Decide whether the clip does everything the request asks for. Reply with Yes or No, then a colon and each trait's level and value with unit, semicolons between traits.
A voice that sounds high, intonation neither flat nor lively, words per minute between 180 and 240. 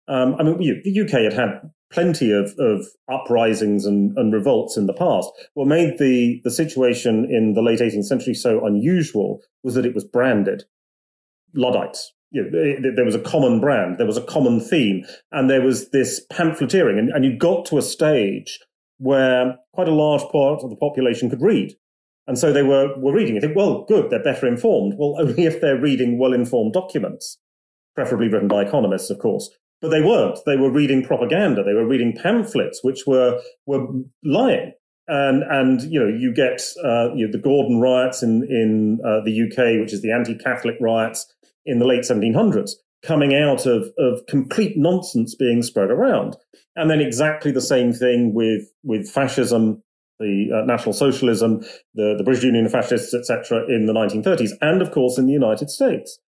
No: low, 130 Hz; average, 4.3 semitones; average, 190 wpm